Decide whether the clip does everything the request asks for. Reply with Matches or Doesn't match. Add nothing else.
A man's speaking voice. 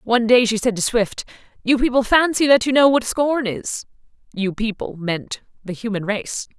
Doesn't match